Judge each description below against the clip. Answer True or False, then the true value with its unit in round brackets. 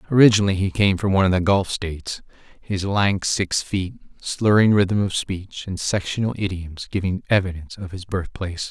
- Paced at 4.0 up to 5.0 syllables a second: False (5.3 syllables/s)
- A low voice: True (95 Hz)